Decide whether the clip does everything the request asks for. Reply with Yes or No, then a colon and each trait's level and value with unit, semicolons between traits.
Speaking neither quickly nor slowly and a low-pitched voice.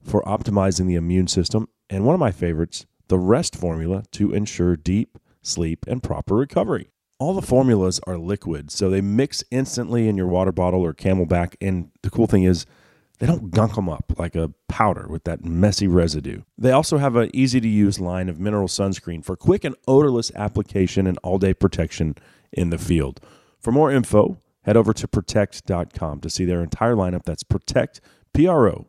Yes: average, 185 wpm; very low, 95 Hz